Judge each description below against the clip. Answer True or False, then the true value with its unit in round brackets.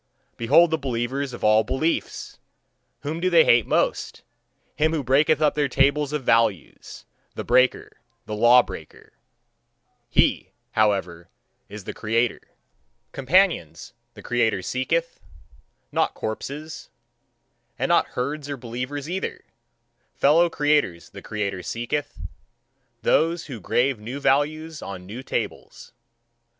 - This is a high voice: False (135 Hz)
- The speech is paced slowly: True (120 wpm)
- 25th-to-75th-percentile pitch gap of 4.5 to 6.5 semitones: True (4.8 semitones)